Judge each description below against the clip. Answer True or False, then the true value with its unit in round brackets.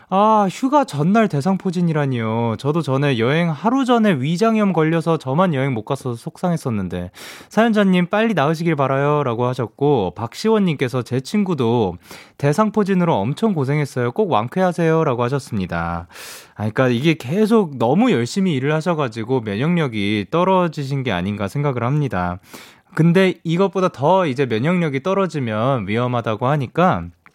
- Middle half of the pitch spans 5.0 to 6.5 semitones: False (7.1 semitones)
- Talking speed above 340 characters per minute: True (355 characters per minute)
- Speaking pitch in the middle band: True (150 Hz)